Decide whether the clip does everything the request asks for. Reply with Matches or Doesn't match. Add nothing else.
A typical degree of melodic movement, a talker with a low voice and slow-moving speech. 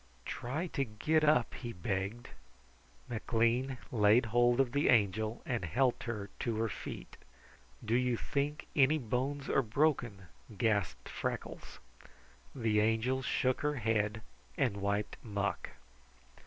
Matches